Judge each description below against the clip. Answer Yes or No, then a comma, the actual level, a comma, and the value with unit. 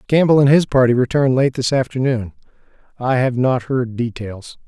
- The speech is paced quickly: No, average, 155 wpm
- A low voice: Yes, low, 130 Hz